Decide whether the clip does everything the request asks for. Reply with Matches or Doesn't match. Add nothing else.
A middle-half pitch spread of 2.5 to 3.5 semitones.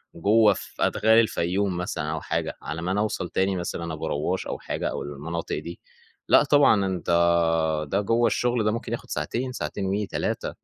Doesn't match